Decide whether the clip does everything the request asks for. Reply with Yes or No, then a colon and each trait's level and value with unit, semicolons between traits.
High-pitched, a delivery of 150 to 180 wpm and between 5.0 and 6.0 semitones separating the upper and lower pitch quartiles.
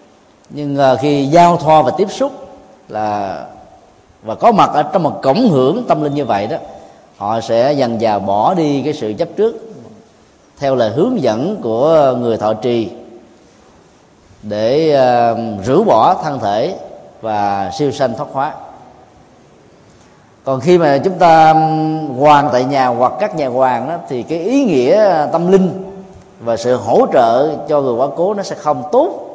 No: medium, 145 Hz; slow, 165 wpm; wide, 5.5 semitones